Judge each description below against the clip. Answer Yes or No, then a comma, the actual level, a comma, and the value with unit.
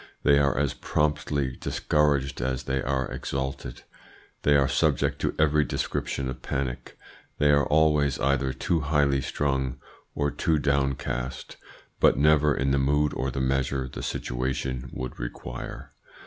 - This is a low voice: Yes, very low, 70 Hz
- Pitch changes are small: Yes, narrow, 1.8 semitones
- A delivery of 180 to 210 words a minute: No, average, 145 wpm